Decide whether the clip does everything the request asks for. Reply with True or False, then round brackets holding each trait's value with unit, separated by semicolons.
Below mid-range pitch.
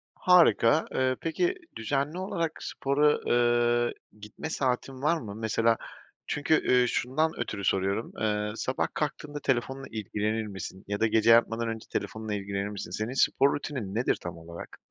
True (120 Hz)